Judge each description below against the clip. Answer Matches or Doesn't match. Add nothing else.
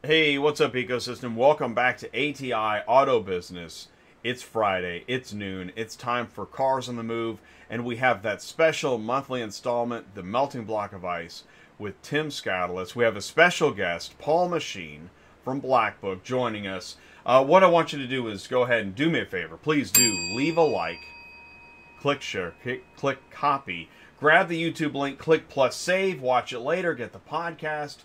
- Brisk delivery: Doesn't match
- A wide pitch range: Matches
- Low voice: Matches